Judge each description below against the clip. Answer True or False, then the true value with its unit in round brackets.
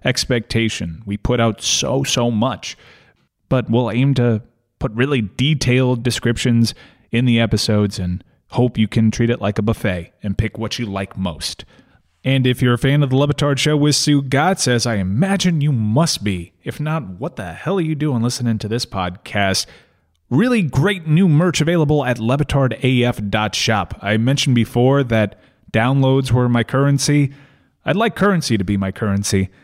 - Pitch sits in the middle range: False (120 Hz)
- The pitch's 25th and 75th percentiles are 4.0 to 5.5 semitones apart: True (4.6 semitones)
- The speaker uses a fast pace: False (170 wpm)